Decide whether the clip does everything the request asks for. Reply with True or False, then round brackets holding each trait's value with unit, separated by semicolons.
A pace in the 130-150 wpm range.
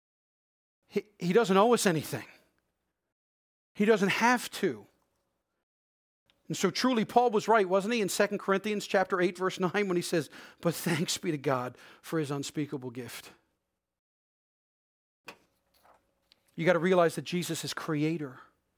True (140 wpm)